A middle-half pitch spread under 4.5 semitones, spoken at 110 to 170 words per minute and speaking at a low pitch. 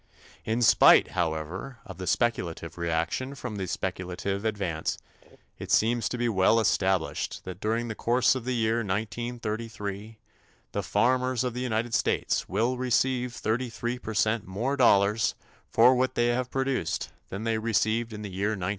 Yes: average, 3.6 semitones; average, 155 wpm; low, 110 Hz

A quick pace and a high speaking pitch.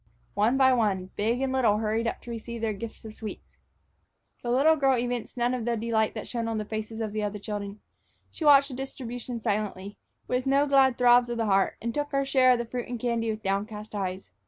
Yes: fast, 230 wpm; high, 230 Hz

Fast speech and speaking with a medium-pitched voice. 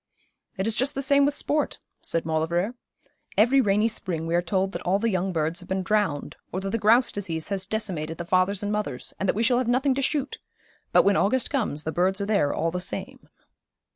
No: fast, 230 wpm; high, 195 Hz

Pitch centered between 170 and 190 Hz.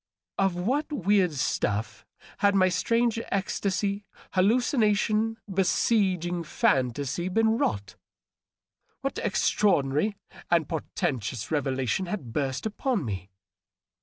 Yes: medium, 185 Hz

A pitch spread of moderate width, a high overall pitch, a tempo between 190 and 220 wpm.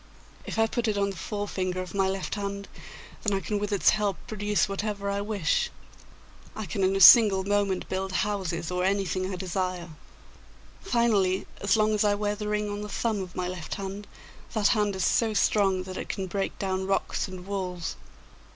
No: narrow, 1.8 semitones; high, 200 Hz; average, 195 wpm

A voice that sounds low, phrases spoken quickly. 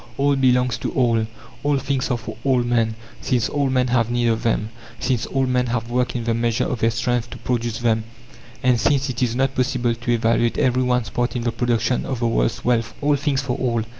Yes: low, 120 Hz; fast, 225 wpm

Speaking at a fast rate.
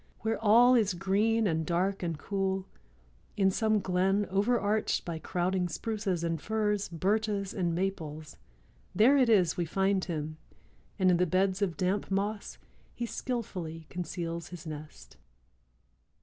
No: average, 140 wpm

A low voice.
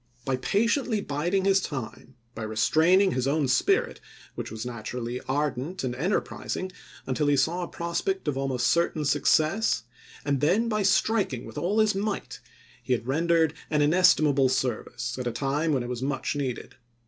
No: medium, 145 Hz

